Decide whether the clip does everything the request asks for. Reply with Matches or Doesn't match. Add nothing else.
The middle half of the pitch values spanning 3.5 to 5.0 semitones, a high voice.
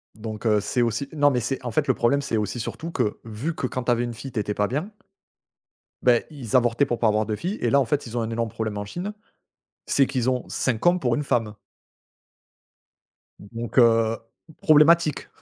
Doesn't match